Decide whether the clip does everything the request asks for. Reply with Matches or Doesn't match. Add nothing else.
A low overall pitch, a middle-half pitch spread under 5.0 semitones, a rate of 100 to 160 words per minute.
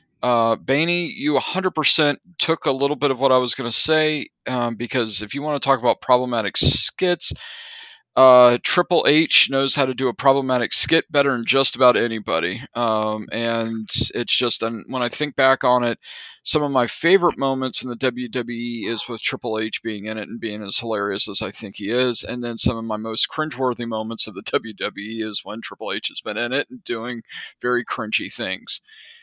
Doesn't match